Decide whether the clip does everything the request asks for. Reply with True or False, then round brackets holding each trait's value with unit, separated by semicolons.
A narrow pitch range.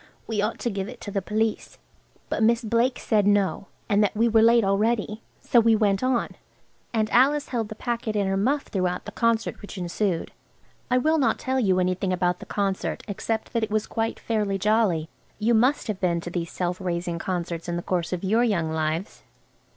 False (3.8 semitones)